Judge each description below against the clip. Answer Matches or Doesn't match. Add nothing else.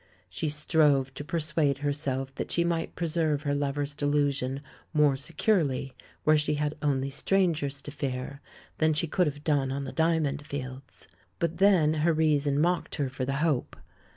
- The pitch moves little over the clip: Matches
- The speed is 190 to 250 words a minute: Doesn't match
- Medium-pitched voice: Matches